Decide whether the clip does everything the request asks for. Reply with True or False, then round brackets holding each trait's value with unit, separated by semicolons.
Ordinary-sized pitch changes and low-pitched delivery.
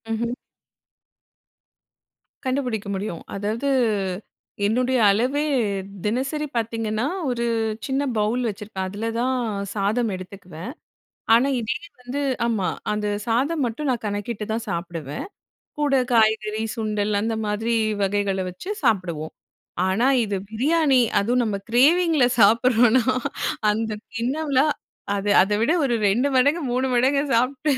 False (3.8 semitones; 230 Hz)